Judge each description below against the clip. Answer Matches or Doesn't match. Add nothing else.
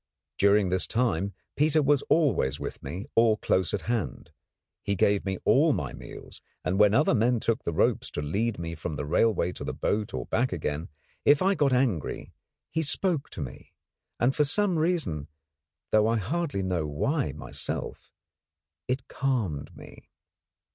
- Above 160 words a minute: Matches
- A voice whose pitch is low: Matches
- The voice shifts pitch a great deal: Matches